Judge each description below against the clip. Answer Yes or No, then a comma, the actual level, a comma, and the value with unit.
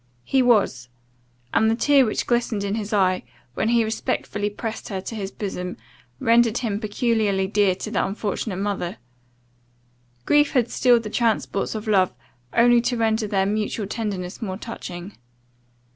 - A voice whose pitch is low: No, high, 215 Hz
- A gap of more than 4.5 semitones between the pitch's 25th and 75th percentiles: No, average, 2.8 semitones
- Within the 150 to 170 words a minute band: Yes, average, 155 wpm